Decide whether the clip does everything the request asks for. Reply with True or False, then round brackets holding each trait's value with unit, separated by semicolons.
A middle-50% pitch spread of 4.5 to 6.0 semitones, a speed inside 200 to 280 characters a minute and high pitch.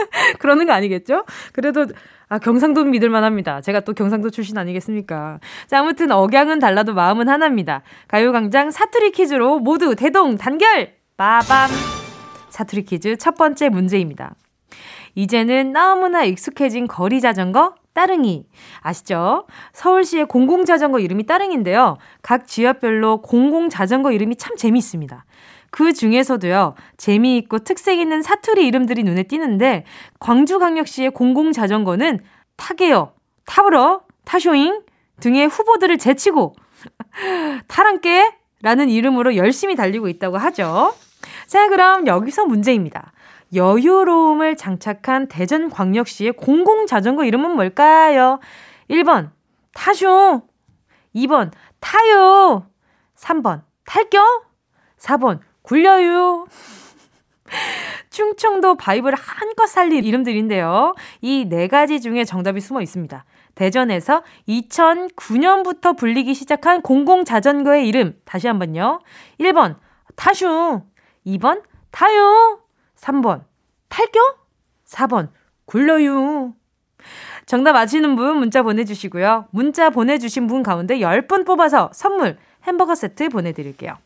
False (7.5 semitones; 270 characters per minute; 270 Hz)